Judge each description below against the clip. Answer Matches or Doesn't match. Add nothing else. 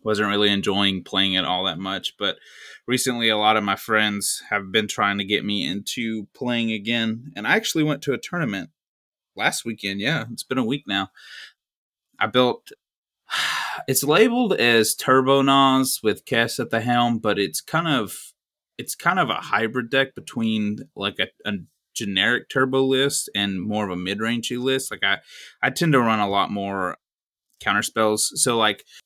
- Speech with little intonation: Doesn't match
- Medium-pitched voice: Doesn't match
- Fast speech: Doesn't match